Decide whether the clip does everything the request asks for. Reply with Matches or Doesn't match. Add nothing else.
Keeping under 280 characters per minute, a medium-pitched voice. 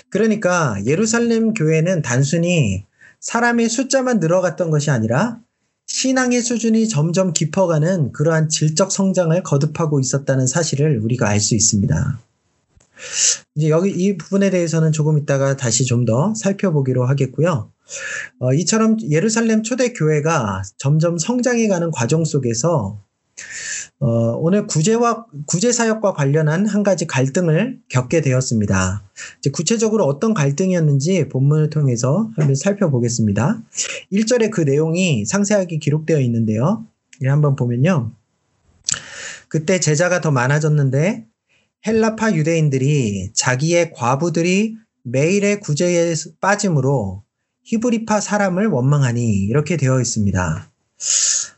Doesn't match